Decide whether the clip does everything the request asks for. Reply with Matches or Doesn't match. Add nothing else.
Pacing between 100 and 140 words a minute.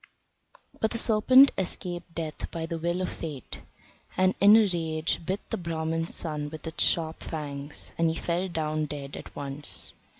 Doesn't match